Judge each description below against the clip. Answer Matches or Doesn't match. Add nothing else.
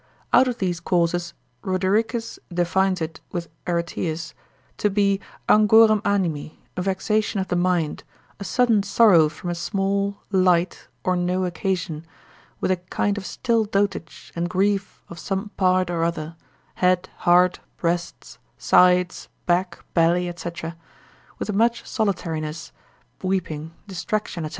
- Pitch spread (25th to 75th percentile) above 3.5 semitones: Doesn't match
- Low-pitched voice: Doesn't match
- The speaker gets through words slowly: Matches